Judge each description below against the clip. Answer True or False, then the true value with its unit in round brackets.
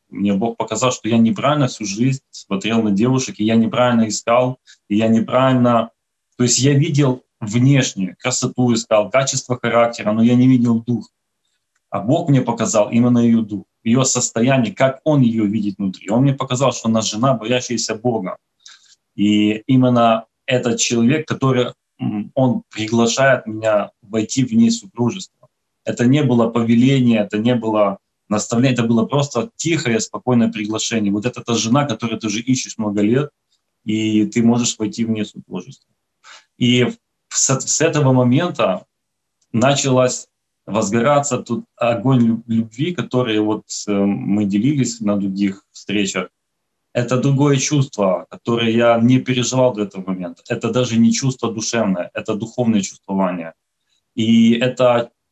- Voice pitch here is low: True (115 Hz)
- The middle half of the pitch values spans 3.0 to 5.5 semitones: False (2.6 semitones)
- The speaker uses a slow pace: False (145 wpm)